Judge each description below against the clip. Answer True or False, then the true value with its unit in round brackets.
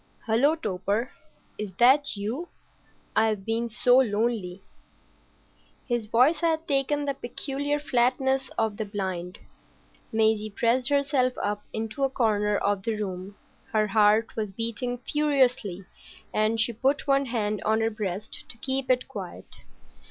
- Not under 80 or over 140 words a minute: True (135 wpm)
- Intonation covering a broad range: False (4.1 semitones)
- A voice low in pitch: False (230 Hz)